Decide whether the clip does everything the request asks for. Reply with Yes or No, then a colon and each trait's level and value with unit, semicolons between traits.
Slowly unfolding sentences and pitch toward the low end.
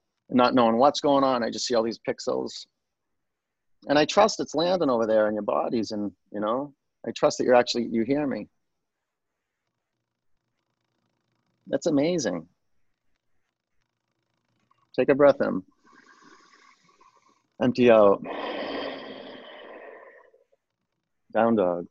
No: slow, 115 wpm; medium, 145 Hz